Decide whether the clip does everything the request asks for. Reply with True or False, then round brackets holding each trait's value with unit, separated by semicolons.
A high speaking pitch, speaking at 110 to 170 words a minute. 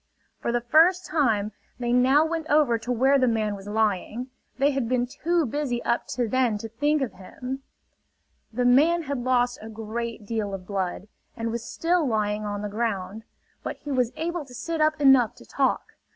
False (245 Hz; 195 wpm)